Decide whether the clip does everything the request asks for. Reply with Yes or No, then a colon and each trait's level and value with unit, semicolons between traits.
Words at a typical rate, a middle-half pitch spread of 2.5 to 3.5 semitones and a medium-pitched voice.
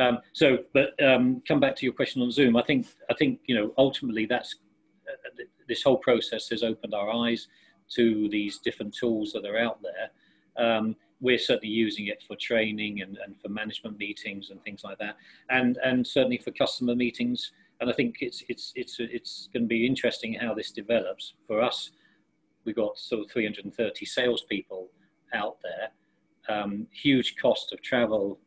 No: average, 185 wpm; average, 3.2 semitones; low, 120 Hz